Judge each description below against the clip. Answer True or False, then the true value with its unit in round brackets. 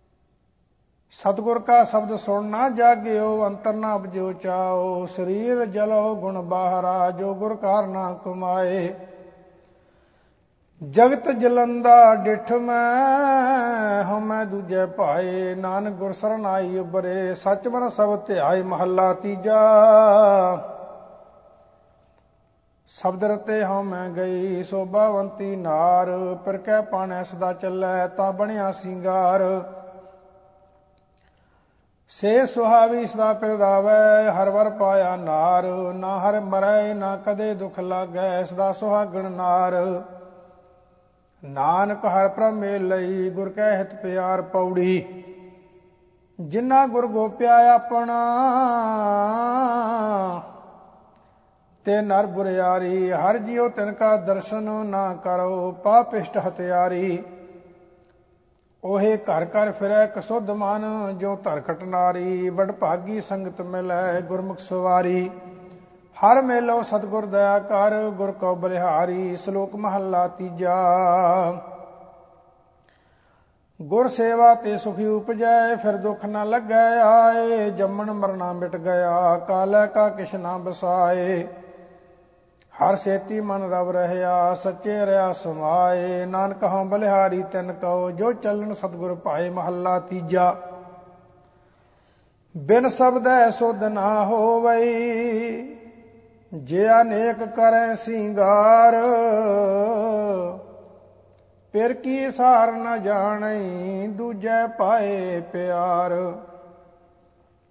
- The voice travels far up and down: False (2.9 semitones)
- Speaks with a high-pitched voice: True (195 Hz)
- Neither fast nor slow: False (95 wpm)